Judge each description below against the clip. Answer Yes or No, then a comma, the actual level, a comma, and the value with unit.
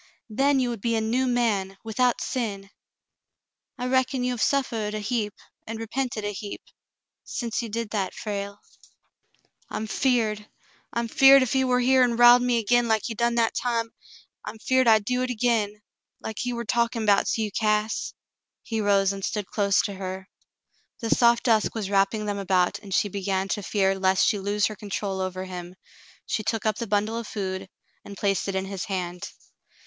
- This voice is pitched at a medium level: No, high, 215 Hz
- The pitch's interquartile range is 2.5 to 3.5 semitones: Yes, average, 3.0 semitones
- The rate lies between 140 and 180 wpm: No, average, 200 wpm